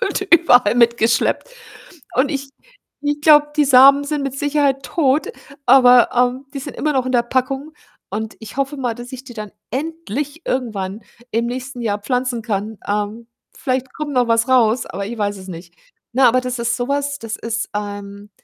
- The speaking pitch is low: No, very high, 250 Hz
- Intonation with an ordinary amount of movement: Yes, average, 3.5 semitones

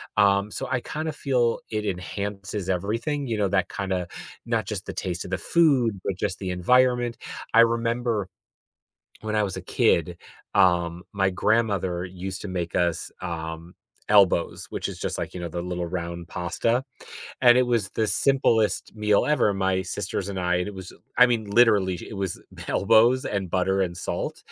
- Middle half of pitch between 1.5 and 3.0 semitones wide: No, average, 4.1 semitones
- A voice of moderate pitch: No, low, 100 Hz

